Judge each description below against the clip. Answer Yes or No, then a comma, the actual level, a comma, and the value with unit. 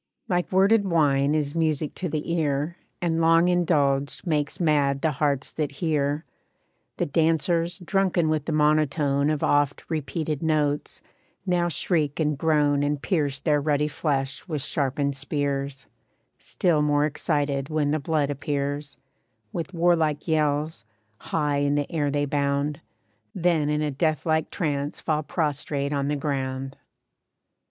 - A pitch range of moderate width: No, narrow, 2.2 semitones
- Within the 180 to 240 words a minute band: No, average, 140 wpm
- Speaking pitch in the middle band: Yes, medium, 150 Hz